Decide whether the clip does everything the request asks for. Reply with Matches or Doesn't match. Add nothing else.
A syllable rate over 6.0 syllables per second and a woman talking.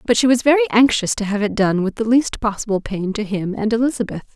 Matches